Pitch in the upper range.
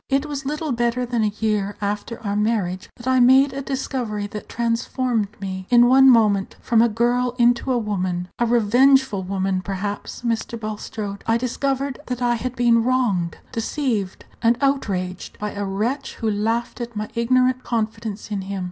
Yes: high, 230 Hz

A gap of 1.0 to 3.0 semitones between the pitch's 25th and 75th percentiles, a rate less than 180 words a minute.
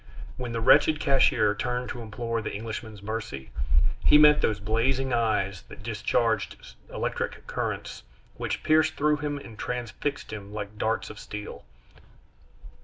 No: average, 4.0 semitones; average, 140 wpm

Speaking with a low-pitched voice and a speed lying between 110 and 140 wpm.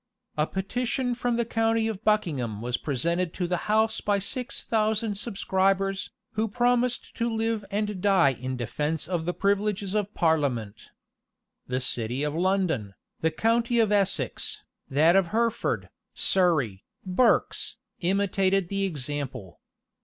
No: high, 195 Hz; slow, 135 wpm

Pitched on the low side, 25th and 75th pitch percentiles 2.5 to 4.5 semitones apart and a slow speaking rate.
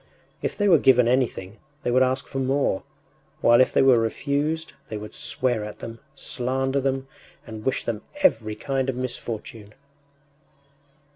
No: low, 130 Hz; average, 2.9 semitones; average, 155 wpm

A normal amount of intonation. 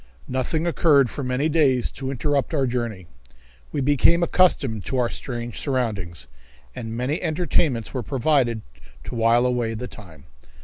Yes: average, 3.7 semitones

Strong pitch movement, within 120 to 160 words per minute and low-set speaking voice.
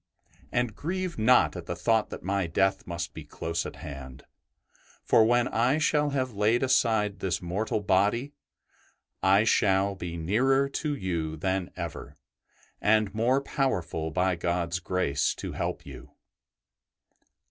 Yes: wide, 5.8 semitones; average, 140 wpm; low, 100 Hz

